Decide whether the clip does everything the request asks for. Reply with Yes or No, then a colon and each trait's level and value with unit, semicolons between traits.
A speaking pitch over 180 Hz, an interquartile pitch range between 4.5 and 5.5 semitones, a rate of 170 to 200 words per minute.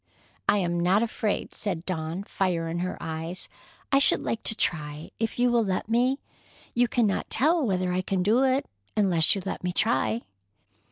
Yes: high, 190 Hz; average, 5.0 semitones; average, 180 wpm